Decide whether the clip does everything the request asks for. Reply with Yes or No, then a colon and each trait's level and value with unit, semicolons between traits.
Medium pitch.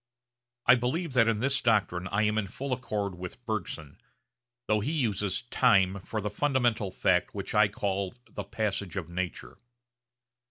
No: low, 105 Hz